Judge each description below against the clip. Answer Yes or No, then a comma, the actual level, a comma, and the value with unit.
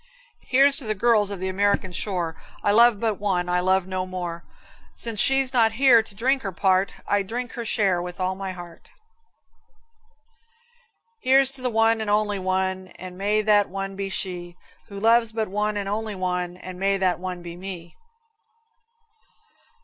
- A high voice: Yes, high, 195 Hz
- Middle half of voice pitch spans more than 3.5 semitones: No, average, 3.1 semitones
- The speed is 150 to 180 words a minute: Yes, average, 170 wpm